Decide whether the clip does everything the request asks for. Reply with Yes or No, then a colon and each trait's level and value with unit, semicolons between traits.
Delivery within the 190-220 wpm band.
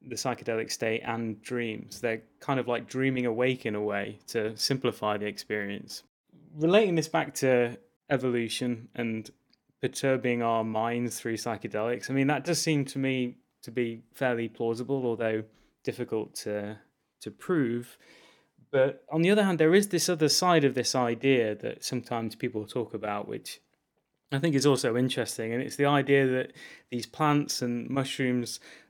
No: average, 160 wpm